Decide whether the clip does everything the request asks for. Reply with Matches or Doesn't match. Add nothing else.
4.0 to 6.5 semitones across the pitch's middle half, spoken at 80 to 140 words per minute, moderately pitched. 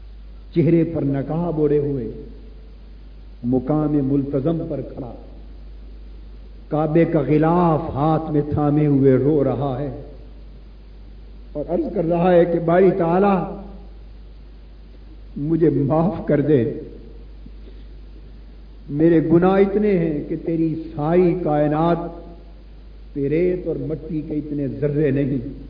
Doesn't match